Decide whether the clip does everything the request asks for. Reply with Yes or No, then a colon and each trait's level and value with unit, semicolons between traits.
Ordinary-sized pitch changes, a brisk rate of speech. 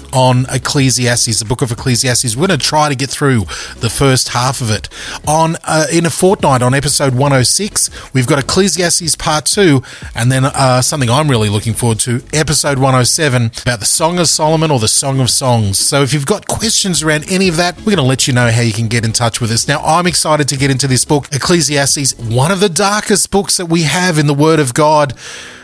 Yes: average, 4.2 semitones; fast, 240 wpm